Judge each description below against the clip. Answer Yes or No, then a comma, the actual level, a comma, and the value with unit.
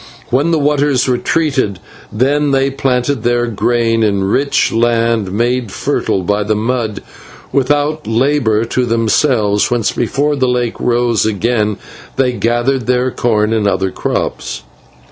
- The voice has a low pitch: Yes, low, 120 Hz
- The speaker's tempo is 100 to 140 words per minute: Yes, slow, 135 wpm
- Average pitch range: Yes, average, 3.4 semitones